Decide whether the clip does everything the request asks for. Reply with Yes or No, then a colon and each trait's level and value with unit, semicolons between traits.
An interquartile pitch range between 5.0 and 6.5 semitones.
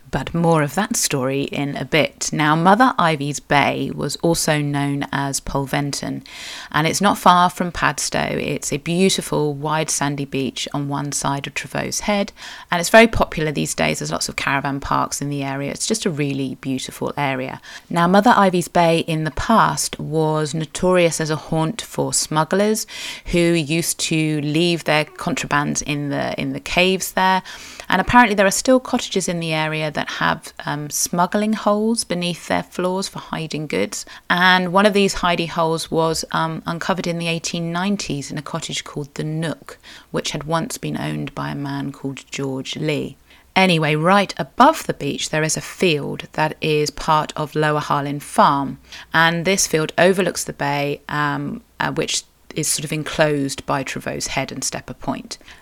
No: average, 4.1 semitones